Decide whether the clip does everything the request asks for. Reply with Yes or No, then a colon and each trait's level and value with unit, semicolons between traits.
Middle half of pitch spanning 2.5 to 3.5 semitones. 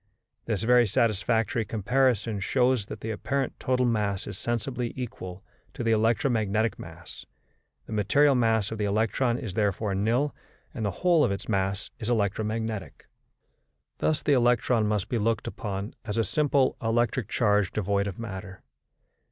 Yes: average, 3.1 semitones